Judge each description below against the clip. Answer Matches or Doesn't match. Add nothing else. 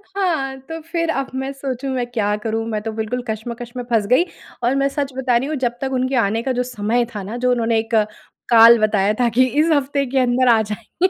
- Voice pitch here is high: Matches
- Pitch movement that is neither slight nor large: Matches